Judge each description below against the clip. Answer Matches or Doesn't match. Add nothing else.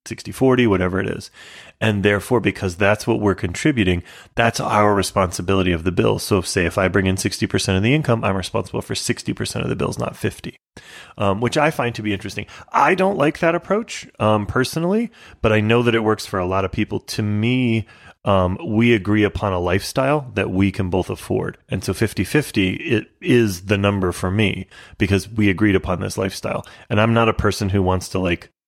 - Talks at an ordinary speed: Doesn't match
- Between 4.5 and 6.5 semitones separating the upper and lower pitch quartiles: Doesn't match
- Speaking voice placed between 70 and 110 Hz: Matches